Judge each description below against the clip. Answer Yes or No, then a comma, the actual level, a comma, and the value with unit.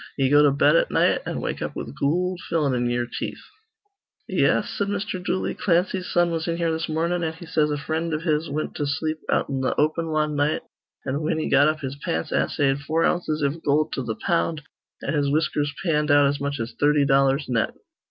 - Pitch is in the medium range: Yes, medium, 150 Hz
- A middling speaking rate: No, fast, 225 wpm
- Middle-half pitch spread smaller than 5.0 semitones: Yes, narrow, 2.6 semitones